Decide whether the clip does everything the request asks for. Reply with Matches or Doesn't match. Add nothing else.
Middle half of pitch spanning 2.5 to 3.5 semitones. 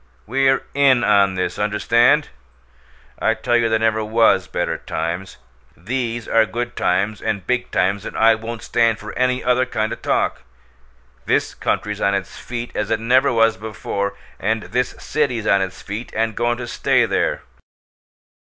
Matches